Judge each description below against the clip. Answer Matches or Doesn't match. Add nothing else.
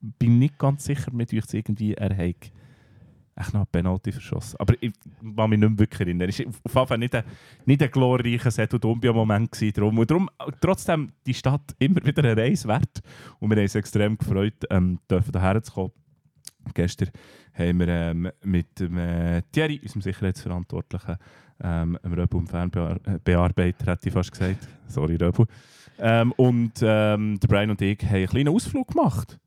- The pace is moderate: Matches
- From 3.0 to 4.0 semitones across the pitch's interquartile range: Doesn't match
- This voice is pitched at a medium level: Doesn't match